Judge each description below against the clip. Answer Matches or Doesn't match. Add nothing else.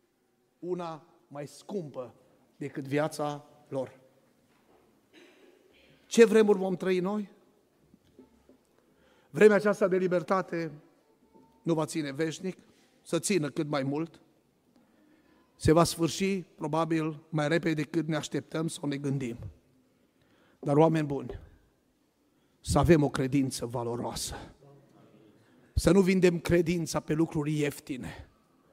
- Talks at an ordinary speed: Doesn't match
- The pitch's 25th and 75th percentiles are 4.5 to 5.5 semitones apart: Doesn't match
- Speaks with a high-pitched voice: Doesn't match